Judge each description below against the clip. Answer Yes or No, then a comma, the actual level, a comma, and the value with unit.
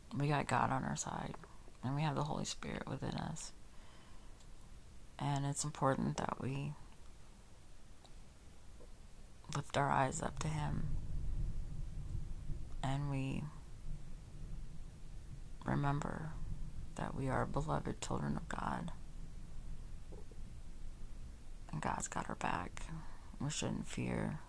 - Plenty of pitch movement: Yes, wide, 8.6 semitones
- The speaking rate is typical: No, slow, 105 wpm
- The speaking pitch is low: Yes, low, 125 Hz